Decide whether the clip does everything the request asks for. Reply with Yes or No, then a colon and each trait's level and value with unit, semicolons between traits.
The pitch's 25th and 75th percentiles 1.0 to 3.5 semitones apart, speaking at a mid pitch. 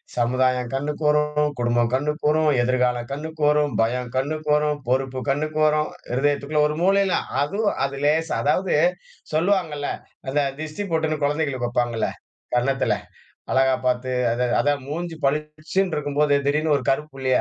Yes: average, 2.8 semitones; medium, 145 Hz